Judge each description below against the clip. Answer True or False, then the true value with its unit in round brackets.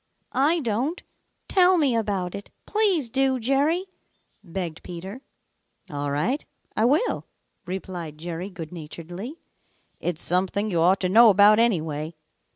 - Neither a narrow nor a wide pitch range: False (7.3 semitones)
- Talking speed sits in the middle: False (130 wpm)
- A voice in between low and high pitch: False (200 Hz)